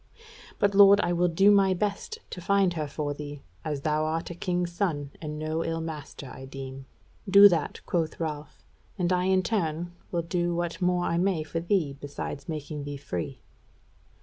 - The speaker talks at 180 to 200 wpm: Yes, average, 185 wpm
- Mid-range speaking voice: Yes, medium, 165 Hz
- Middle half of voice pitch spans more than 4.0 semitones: No, average, 3.3 semitones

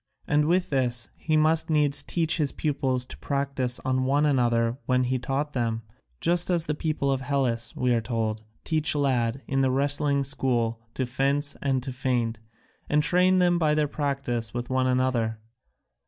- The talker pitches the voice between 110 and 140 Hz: Yes, low, 135 Hz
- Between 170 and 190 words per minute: Yes, average, 175 wpm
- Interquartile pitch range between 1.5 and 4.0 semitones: Yes, average, 3.2 semitones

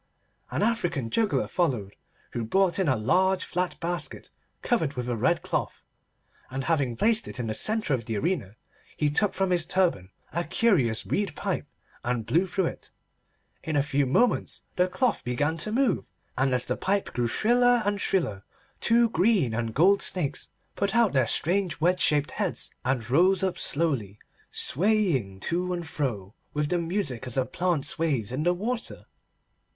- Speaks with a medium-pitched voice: Yes, medium, 165 Hz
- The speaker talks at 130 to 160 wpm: No, average, 175 wpm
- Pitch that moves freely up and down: Yes, wide, 7.3 semitones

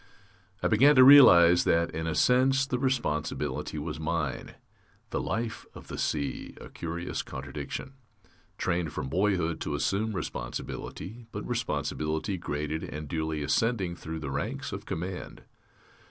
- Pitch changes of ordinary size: No, wide, 6.2 semitones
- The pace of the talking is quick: No, average, 140 wpm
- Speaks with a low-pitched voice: Yes, very low, 85 Hz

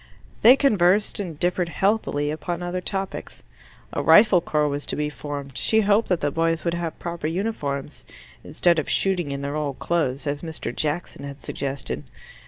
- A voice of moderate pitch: Yes, medium, 165 Hz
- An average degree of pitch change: Yes, average, 4.0 semitones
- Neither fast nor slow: Yes, average, 175 wpm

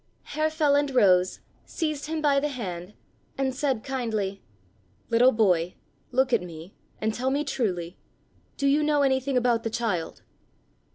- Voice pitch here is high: Yes, very high, 250 Hz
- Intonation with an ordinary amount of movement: No, wide, 5.9 semitones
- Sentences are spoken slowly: No, average, 150 wpm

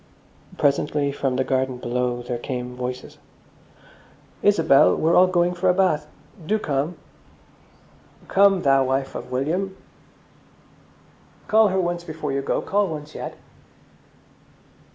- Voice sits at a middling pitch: Yes, medium, 150 Hz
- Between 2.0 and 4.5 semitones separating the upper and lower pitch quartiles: No, wide, 5.4 semitones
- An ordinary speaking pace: No, slow, 125 wpm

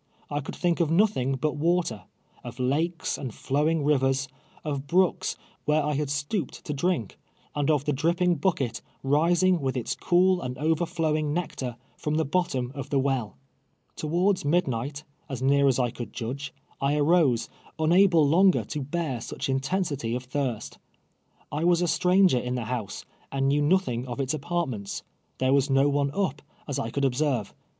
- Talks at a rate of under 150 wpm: No, average, 175 wpm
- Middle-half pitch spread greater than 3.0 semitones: Yes, average, 4.2 semitones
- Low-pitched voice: No, medium, 145 Hz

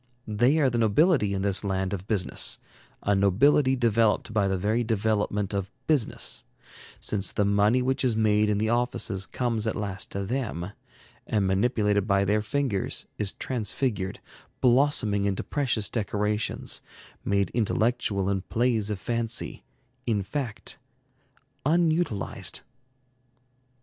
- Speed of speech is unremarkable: No, slow, 130 wpm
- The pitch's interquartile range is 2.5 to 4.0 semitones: Yes, average, 3.4 semitones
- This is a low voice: Yes, low, 105 Hz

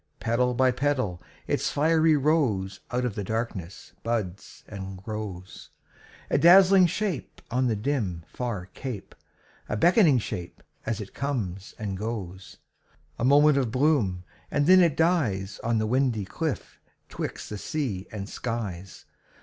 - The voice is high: No, low, 115 Hz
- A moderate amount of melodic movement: No, wide, 6.6 semitones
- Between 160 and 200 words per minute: No, average, 140 wpm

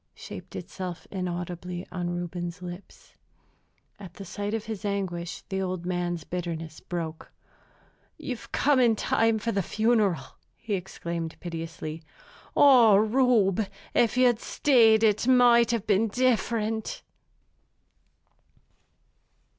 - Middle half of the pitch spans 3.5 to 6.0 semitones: Yes, average, 4.5 semitones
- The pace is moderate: No, slow, 115 wpm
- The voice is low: No, high, 195 Hz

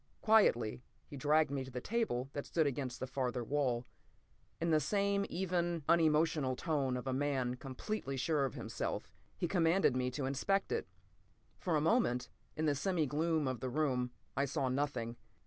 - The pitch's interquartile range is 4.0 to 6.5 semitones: Yes, average, 4.4 semitones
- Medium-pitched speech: Yes, medium, 145 Hz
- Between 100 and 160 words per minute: No, average, 175 wpm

